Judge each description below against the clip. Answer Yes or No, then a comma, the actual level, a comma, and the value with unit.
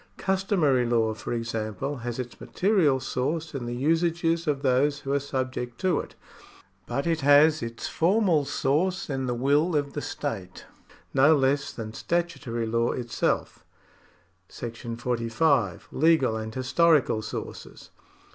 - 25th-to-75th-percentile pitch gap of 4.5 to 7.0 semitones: Yes, average, 5.0 semitones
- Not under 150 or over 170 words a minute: No, slow, 135 wpm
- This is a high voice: No, low, 135 Hz